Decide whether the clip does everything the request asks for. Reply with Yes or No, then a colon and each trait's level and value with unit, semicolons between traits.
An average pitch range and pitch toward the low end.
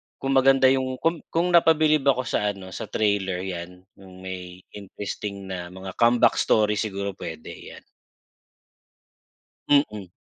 No: wide, 6.1 semitones; low, 105 Hz